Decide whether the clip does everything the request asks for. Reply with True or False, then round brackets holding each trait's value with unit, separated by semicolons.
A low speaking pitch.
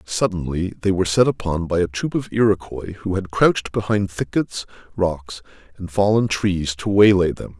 True (95 Hz)